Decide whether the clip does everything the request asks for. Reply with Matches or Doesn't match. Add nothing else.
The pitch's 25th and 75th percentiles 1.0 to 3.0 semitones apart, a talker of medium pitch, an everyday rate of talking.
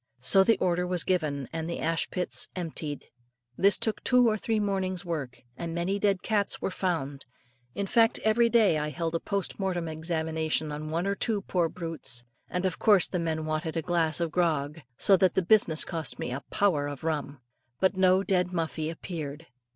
Doesn't match